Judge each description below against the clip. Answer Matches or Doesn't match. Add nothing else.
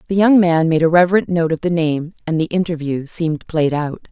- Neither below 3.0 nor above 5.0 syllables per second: Doesn't match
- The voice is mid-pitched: Matches